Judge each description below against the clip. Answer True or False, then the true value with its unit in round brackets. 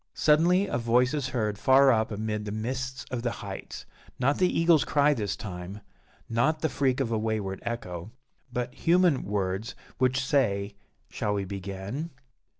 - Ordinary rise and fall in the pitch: True (4.9 semitones)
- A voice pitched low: True (120 Hz)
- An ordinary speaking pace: True (160 wpm)